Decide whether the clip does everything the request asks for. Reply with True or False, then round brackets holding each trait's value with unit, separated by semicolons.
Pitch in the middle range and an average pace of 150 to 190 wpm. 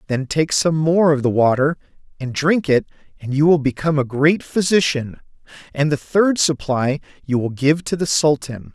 True (145 Hz; 185 wpm)